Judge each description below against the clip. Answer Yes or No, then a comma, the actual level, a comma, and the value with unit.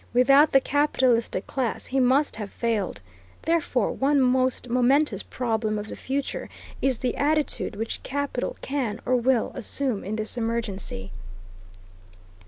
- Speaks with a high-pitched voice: Yes, very high, 250 Hz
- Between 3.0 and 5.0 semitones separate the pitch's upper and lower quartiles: Yes, average, 3.5 semitones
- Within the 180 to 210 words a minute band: No, slow, 135 wpm